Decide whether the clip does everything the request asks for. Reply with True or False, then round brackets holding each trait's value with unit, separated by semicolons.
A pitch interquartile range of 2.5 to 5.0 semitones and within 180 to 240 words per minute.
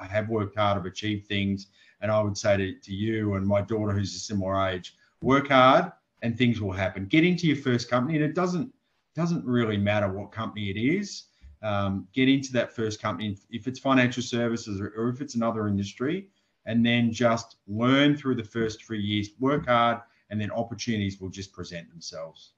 True (3.6 semitones; 200 wpm)